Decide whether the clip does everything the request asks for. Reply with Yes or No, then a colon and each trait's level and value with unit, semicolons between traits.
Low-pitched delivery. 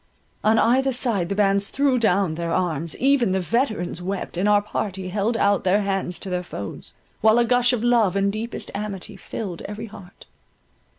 No: high, 205 Hz